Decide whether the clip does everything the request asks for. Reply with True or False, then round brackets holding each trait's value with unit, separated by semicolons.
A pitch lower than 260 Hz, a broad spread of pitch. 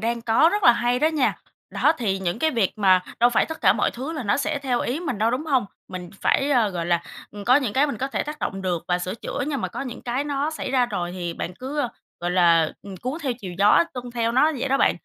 True (240 Hz; 6.4 semitones)